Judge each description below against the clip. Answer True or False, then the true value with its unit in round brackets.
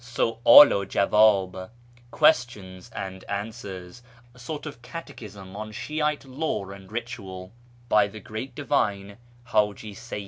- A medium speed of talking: False (125 wpm)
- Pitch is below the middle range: True (110 Hz)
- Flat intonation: False (3.9 semitones)